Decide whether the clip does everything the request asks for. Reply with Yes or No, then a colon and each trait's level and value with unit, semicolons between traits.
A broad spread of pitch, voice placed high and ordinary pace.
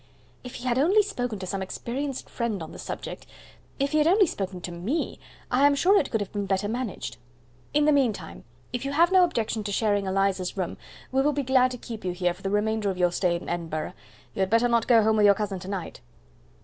No: wide, 5.8 semitones; high, 220 Hz; fast, 240 wpm